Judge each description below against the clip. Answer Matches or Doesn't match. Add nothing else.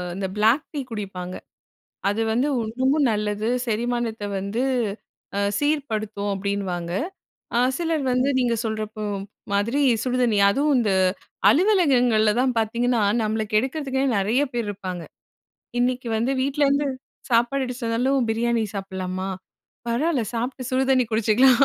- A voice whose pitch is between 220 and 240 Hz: Matches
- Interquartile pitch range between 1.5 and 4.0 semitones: Matches